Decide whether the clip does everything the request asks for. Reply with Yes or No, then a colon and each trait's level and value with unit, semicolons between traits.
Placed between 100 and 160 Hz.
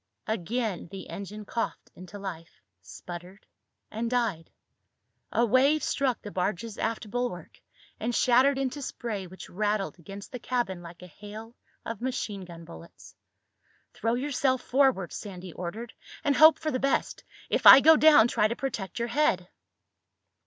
No: high, 220 Hz